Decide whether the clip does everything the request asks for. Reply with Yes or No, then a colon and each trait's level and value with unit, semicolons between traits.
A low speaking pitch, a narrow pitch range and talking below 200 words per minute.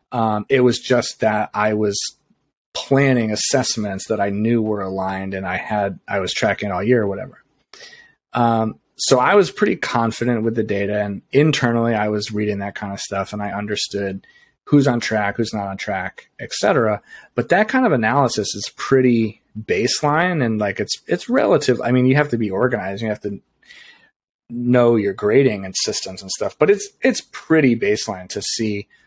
No: low, 110 Hz; average, 3.3 semitones; average, 185 wpm